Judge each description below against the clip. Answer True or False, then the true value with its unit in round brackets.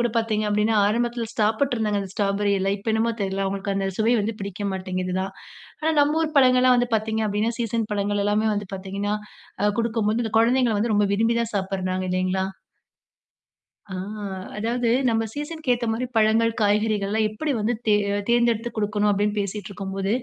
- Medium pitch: False (215 Hz)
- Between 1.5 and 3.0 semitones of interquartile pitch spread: True (2.6 semitones)